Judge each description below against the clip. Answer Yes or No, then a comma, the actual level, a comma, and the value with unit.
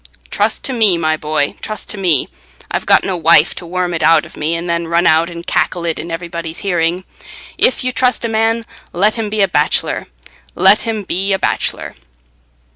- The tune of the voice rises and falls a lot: No, average, 3.8 semitones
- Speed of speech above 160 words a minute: Yes, average, 200 wpm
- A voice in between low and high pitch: Yes, medium, 175 Hz